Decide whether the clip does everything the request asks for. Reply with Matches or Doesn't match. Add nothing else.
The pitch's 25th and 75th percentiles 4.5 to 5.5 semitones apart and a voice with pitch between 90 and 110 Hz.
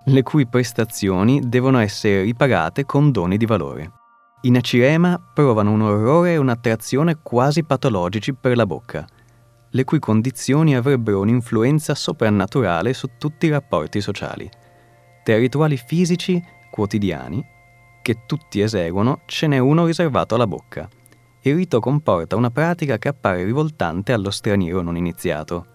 Doesn't match